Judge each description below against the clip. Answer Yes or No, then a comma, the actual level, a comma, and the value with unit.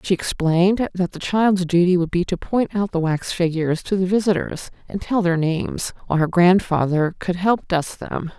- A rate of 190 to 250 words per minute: Yes, average, 200 wpm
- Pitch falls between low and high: Yes, medium, 180 Hz